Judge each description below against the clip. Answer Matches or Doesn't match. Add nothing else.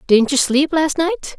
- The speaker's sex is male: Doesn't match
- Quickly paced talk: Matches